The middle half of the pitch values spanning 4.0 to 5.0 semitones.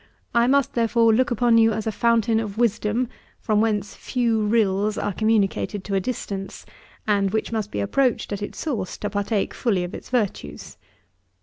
No: narrow, 2.4 semitones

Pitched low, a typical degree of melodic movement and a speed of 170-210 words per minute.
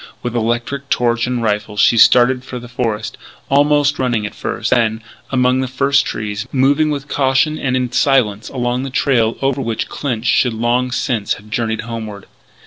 Yes: low, 125 Hz; average, 3.1 semitones; average, 175 wpm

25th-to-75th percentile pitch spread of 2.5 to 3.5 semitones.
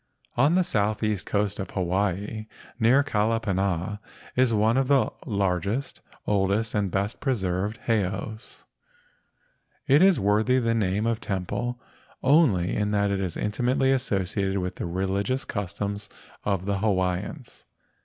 Yes: average, 3.1 semitones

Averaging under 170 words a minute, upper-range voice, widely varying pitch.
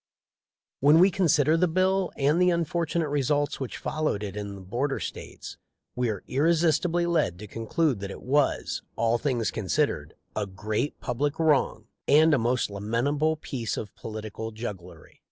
No: average, 160 wpm; medium, 140 Hz; wide, 6.6 semitones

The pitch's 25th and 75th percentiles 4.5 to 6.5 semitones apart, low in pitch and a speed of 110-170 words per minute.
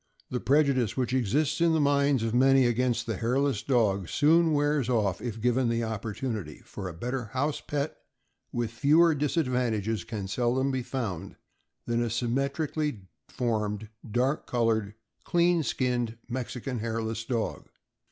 No: average, 3.7 semitones; low, 125 Hz; average, 140 wpm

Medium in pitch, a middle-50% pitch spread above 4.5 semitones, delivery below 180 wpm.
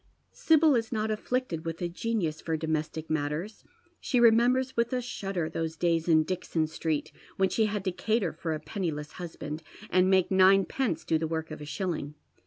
No: medium, 175 Hz; average, 5.3 semitones; average, 185 wpm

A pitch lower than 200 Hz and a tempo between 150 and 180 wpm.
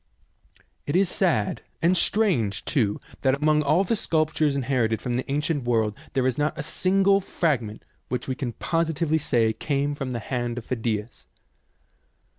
Yes: medium, 140 Hz; average, 160 wpm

